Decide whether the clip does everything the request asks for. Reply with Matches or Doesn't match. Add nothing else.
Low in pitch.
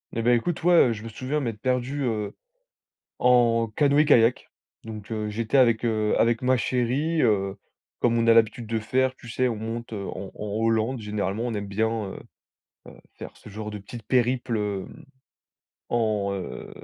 Matches